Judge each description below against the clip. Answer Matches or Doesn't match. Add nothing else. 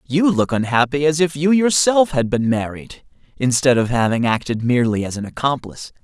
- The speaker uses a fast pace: Doesn't match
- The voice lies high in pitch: Doesn't match